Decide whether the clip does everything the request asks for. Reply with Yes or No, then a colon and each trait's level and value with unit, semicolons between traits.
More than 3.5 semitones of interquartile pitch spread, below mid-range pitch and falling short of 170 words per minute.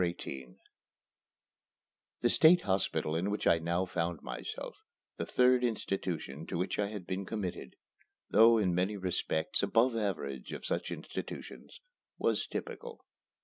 Yes: average, 4.2 semitones; very low, 95 Hz; average, 140 wpm